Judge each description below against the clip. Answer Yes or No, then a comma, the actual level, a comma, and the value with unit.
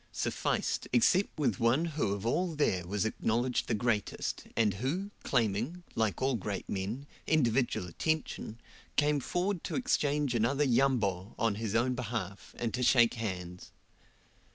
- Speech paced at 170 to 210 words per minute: No, average, 145 wpm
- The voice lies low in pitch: Yes, low, 120 Hz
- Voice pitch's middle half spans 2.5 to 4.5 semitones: No, average, 5.3 semitones